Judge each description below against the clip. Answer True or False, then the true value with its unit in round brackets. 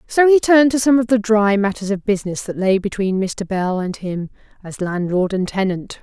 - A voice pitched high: True (205 Hz)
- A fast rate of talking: True (220 wpm)